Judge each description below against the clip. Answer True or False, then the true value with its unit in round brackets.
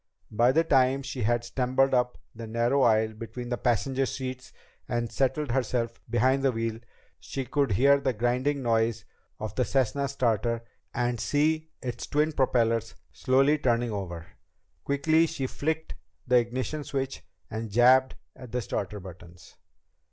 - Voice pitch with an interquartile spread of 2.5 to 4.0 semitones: True (2.9 semitones)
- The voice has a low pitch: True (125 Hz)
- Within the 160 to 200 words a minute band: False (150 wpm)